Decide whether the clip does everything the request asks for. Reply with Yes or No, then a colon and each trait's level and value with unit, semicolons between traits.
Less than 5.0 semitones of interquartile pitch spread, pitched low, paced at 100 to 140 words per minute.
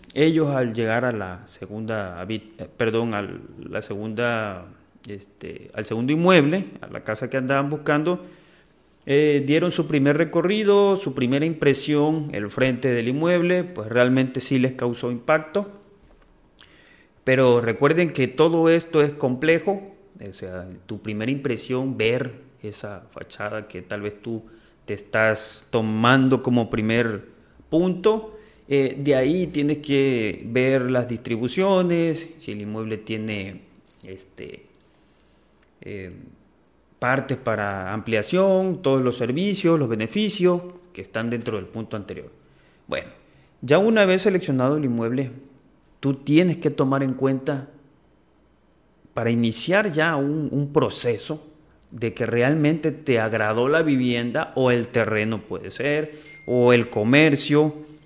No: wide, 5.5 semitones; low, 130 Hz; average, 130 wpm